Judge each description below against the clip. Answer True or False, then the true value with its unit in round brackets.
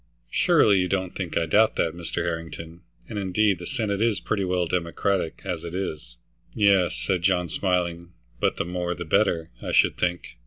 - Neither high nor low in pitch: False (90 Hz)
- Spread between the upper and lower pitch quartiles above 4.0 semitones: False (2.4 semitones)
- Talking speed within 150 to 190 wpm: True (185 wpm)